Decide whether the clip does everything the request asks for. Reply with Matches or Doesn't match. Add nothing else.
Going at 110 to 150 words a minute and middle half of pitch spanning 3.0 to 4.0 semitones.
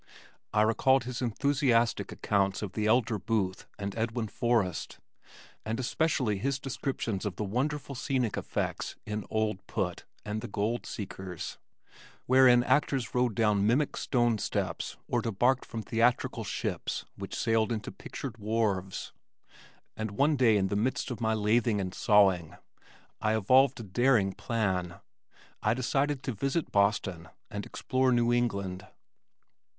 Matches